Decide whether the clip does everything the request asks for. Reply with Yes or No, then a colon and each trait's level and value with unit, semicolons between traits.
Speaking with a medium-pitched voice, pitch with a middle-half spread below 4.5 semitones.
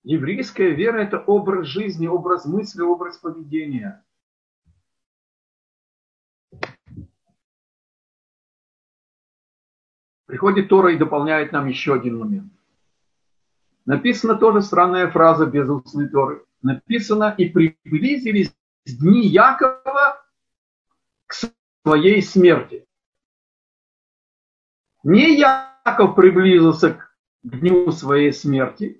No: medium, 180 Hz; wide, 5.4 semitones